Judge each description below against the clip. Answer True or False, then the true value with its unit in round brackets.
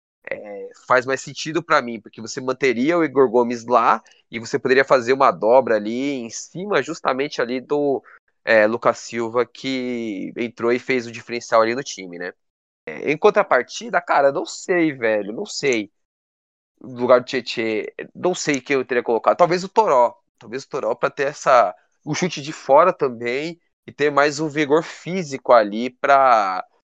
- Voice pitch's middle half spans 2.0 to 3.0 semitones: False (5.2 semitones)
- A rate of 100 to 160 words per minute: False (180 wpm)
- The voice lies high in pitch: False (135 Hz)